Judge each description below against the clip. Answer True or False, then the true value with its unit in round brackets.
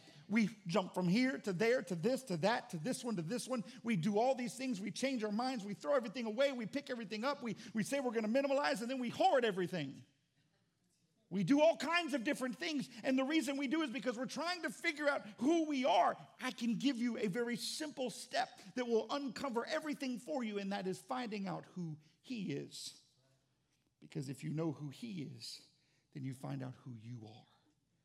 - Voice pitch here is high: True (230 Hz)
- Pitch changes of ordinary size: False (8.1 semitones)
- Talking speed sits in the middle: False (220 wpm)